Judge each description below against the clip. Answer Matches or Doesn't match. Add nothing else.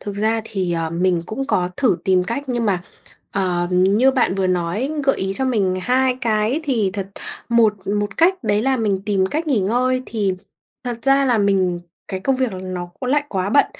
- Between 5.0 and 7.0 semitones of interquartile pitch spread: Matches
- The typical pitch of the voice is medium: Doesn't match